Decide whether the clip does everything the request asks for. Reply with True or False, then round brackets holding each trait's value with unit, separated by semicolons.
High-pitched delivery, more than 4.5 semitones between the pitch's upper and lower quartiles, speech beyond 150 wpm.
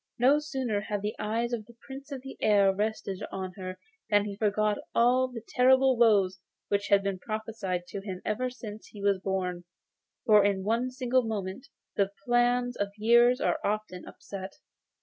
False (215 Hz; 3.6 semitones; 175 wpm)